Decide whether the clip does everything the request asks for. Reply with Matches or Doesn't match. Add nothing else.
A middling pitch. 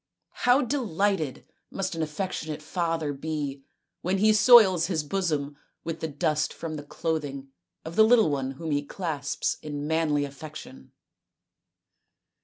Matches